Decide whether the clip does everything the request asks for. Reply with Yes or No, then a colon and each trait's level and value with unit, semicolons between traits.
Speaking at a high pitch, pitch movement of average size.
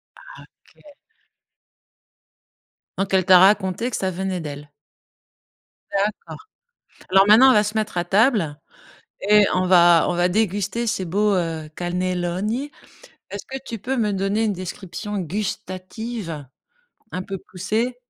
Yes: high, 195 Hz; average, 3.2 semitones